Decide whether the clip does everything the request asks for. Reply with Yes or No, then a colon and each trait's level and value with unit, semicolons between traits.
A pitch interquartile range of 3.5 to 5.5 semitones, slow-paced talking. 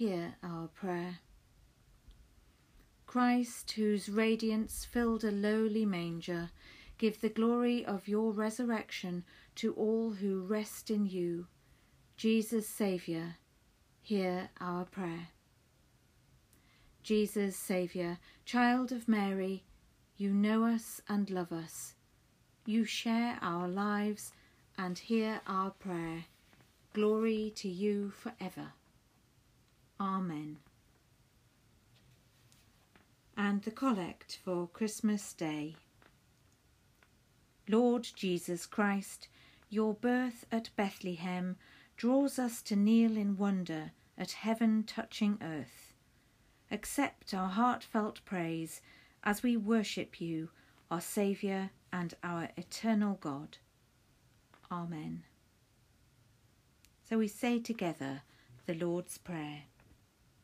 Yes: average, 4.7 semitones; slow, 95 wpm